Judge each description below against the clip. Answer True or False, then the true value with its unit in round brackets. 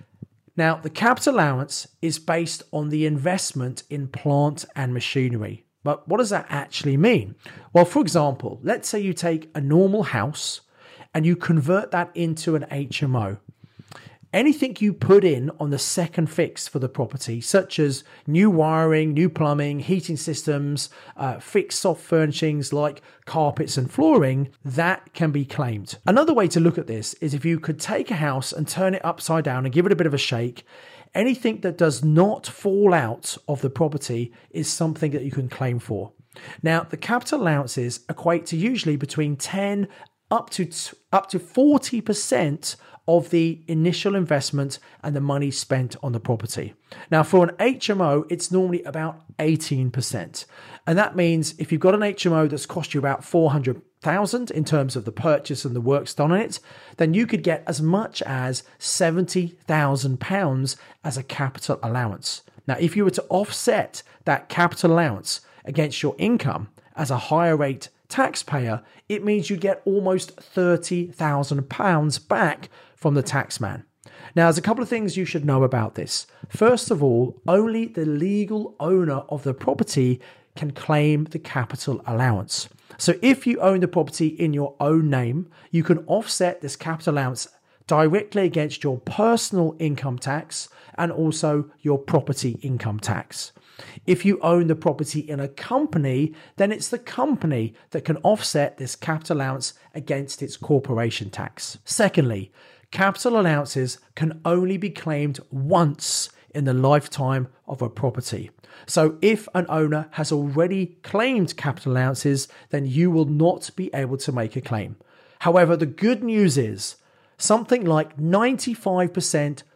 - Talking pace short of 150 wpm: False (160 wpm)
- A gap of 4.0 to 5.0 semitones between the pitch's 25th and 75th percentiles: True (4.5 semitones)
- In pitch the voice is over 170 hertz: False (155 Hz)